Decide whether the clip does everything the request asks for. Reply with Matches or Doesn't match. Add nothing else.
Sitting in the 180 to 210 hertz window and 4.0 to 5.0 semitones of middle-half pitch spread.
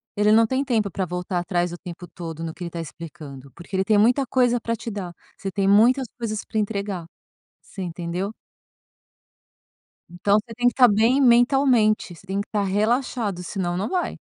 Matches